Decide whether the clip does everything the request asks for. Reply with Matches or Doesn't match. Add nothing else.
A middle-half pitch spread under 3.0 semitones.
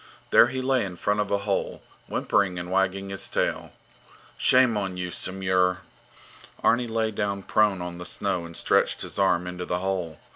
Matches